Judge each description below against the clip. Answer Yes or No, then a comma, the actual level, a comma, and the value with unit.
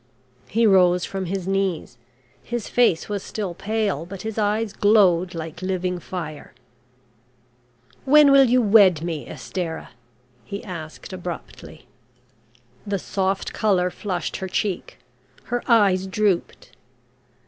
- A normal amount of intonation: Yes, average, 3.2 semitones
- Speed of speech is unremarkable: No, slow, 120 wpm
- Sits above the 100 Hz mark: Yes, high, 190 Hz